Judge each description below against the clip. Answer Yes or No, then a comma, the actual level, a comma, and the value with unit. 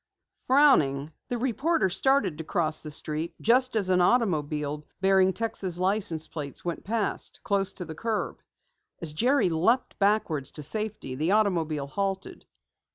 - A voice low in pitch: No, medium, 185 Hz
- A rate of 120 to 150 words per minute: Yes, average, 145 wpm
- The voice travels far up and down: Yes, wide, 5.9 semitones